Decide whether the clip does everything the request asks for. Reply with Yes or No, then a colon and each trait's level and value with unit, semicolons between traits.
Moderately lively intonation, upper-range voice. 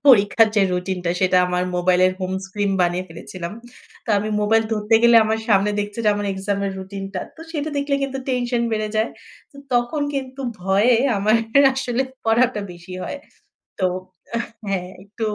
Yes: average, 4.1 semitones; high, 210 Hz